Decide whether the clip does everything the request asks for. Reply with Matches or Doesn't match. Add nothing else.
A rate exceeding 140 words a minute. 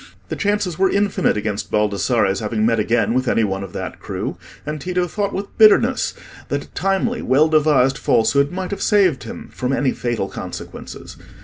Matches